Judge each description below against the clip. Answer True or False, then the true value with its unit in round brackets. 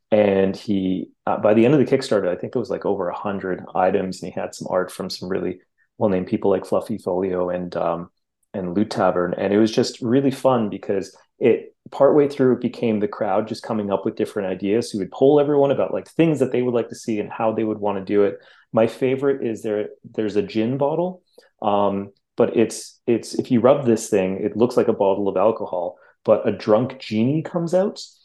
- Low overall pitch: True (110 Hz)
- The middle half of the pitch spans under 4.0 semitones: False (4.8 semitones)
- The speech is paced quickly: True (225 wpm)